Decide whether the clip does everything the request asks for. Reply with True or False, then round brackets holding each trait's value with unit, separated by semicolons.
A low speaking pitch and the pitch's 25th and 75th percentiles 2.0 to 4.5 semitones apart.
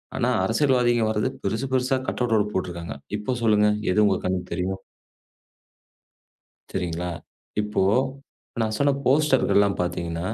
False (105 Hz; 5.0 semitones)